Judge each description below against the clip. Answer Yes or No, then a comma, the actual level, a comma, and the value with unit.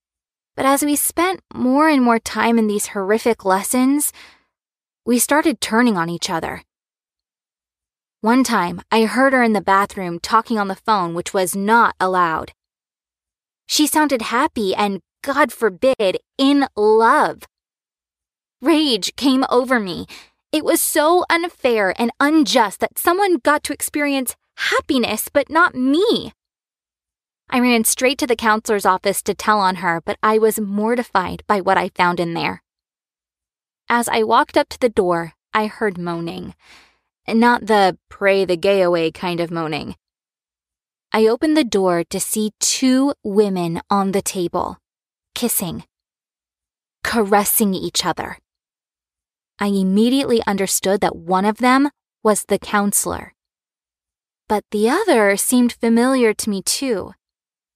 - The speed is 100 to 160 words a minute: Yes, average, 140 wpm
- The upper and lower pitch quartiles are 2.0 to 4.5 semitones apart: No, average, 5.0 semitones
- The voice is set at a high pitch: Yes, high, 220 Hz